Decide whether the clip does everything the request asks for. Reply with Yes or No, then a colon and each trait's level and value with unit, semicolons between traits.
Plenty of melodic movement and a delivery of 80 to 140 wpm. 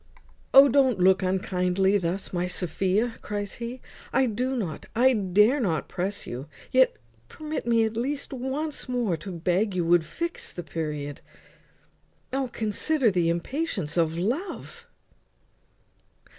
Yes: wide, 6.4 semitones; slow, 135 wpm